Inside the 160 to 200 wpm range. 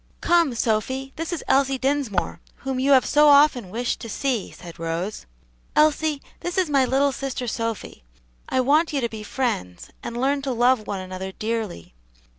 Yes: average, 175 wpm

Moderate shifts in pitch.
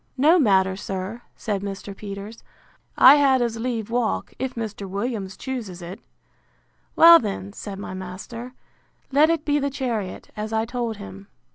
Yes: average, 4.4 semitones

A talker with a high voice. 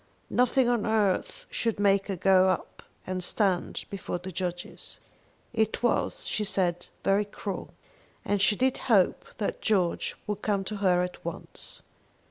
Yes: high, 195 Hz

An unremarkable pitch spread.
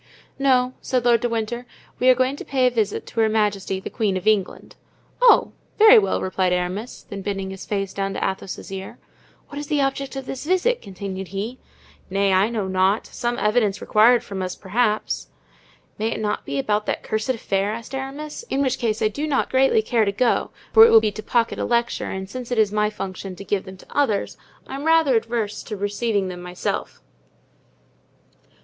Yes: average, 4.3 semitones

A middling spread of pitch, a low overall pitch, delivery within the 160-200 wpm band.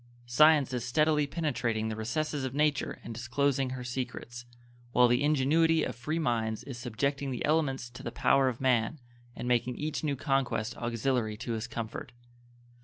Yes: average, 3.3 semitones; low, 130 Hz; average, 170 wpm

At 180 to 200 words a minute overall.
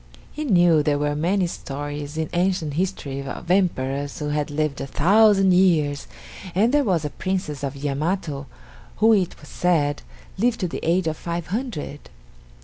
No: average, 165 wpm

